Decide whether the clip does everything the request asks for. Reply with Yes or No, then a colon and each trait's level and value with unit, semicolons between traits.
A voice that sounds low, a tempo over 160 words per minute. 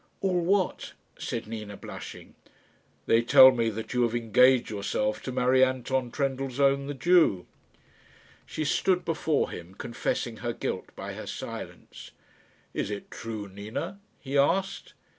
No: low, 125 Hz; average, 140 wpm